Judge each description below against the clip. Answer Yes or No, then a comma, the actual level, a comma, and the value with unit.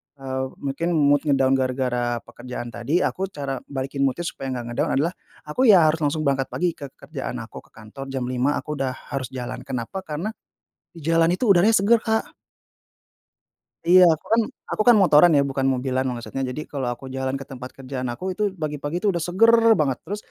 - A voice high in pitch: No, medium, 140 Hz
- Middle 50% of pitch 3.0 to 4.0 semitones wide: No, average, 4.6 semitones